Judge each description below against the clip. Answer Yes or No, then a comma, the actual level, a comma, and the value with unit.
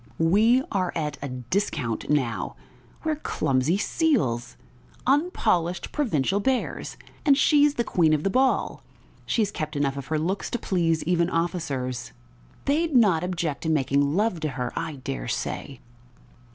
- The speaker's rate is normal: Yes, average, 150 wpm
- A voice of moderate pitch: Yes, medium, 165 Hz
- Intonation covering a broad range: Yes, wide, 7.5 semitones